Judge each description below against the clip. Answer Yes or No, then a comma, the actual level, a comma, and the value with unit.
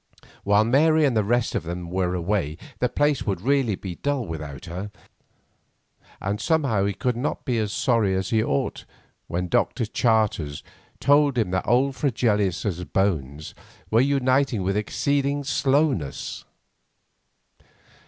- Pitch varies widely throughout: Yes, wide, 6.5 semitones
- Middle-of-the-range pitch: No, low, 110 Hz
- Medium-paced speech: Yes, average, 145 wpm